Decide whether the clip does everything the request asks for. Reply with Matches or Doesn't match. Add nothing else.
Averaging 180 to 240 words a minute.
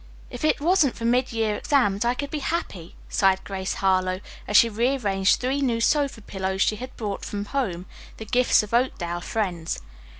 Matches